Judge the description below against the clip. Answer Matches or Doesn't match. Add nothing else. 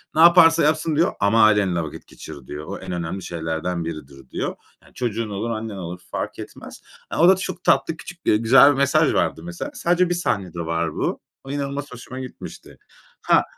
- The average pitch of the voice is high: Doesn't match